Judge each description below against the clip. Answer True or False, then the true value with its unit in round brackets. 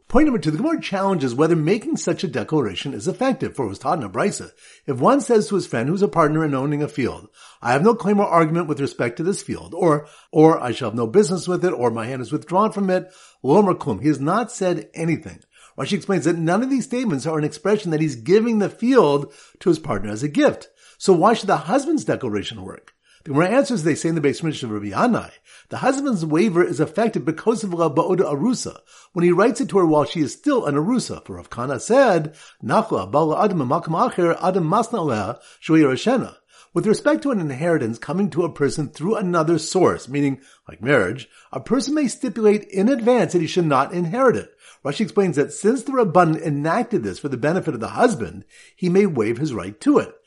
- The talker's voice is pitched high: False (175 Hz)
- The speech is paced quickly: True (215 wpm)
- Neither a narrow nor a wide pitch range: False (6.0 semitones)